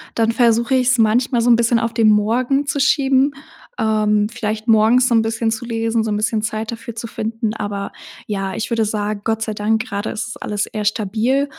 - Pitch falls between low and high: No, high, 225 Hz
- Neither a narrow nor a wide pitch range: No, narrow, 1.8 semitones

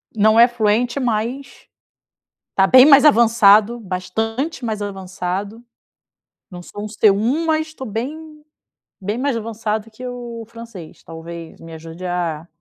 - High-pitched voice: Yes, high, 220 Hz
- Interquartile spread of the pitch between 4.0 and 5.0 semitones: Yes, average, 4.3 semitones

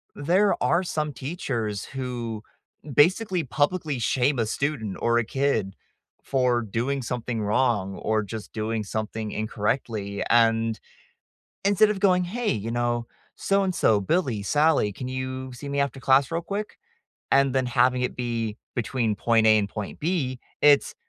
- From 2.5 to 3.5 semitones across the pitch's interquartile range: No, average, 4.6 semitones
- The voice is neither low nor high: No, low, 125 Hz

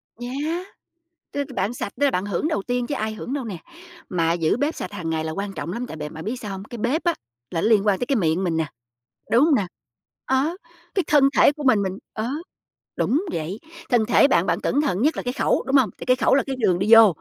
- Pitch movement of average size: No, wide, 6.3 semitones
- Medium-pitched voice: No, high, 225 Hz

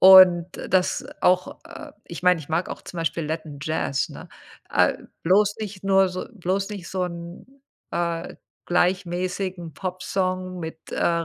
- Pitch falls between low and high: Yes, medium, 180 Hz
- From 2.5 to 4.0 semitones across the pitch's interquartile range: No, narrow, 1.8 semitones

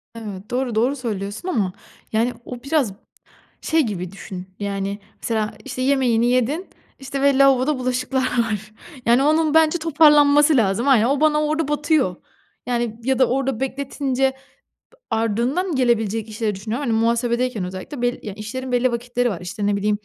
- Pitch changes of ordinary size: Yes, average, 4.0 semitones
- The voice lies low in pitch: No, high, 245 Hz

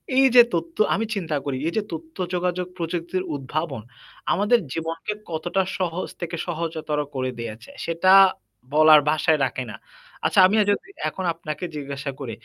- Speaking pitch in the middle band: Yes, medium, 165 Hz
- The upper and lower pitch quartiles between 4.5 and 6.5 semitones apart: No, average, 3.3 semitones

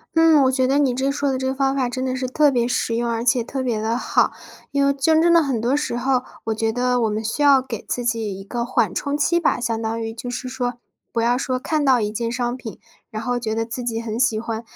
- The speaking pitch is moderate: No, high, 245 Hz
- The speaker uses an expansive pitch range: No, average, 2.7 semitones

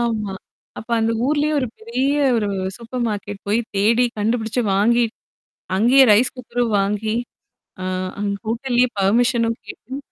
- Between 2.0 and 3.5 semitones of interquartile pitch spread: Yes, average, 2.8 semitones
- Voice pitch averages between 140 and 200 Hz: No, high, 230 Hz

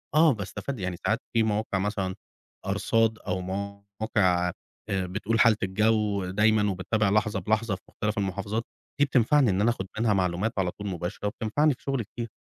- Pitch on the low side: Yes, low, 105 Hz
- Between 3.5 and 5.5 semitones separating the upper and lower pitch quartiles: No, average, 2.7 semitones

